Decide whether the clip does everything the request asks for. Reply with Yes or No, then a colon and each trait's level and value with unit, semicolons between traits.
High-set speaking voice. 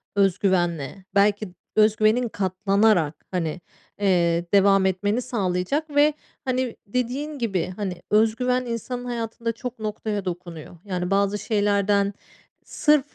Yes: high, 205 Hz